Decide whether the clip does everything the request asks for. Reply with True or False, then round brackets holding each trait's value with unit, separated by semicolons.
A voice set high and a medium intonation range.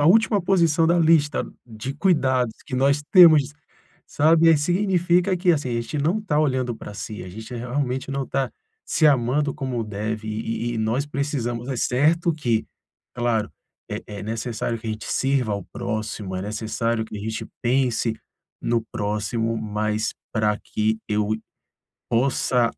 False (125 Hz; 5.0 semitones)